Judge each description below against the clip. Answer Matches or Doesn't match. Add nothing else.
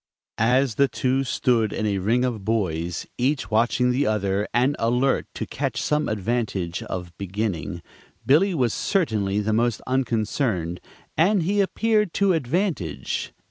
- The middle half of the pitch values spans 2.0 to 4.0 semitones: Doesn't match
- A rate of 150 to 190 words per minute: Doesn't match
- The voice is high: Doesn't match